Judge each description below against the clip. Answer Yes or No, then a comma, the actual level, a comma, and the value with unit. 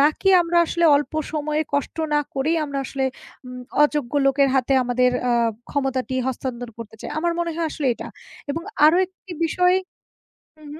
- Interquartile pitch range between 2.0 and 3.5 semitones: No, average, 3.9 semitones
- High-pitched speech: Yes, very high, 285 Hz